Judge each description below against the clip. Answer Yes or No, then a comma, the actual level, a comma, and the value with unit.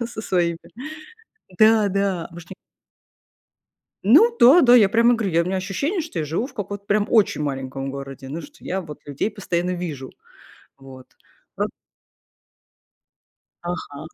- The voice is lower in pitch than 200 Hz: Yes, medium, 185 Hz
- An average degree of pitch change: No, wide, 6.1 semitones